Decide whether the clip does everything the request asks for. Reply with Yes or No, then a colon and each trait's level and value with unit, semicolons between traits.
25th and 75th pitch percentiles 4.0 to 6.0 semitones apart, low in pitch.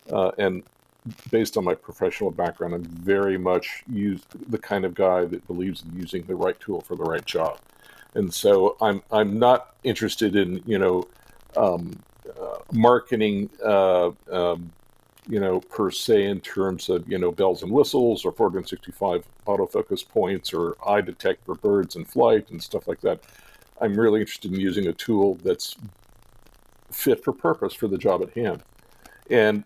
Yes: average, 4.3 semitones; low, 100 Hz